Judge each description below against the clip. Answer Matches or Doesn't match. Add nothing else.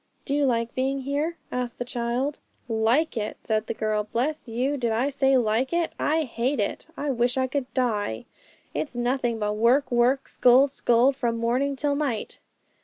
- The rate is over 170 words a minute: Matches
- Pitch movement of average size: Matches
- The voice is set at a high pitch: Matches